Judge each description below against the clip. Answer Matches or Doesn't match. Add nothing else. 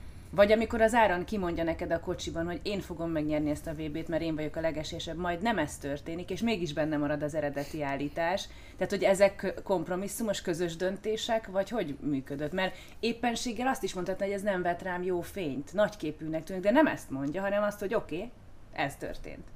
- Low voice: Doesn't match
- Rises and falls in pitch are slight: Doesn't match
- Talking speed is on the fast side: Matches